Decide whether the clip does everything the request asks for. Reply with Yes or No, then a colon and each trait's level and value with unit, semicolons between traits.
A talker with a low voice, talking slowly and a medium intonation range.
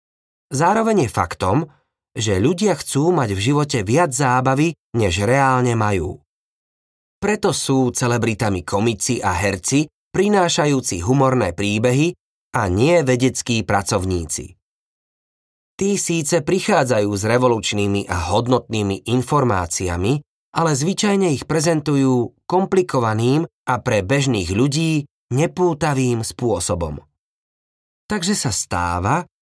No: low, 125 Hz; slow, 100 wpm; wide, 7.6 semitones